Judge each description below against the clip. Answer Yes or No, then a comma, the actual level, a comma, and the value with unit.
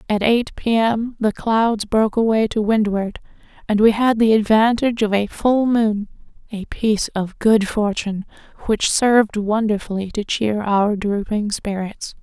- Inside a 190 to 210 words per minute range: No, average, 150 wpm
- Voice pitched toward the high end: Yes, high, 215 Hz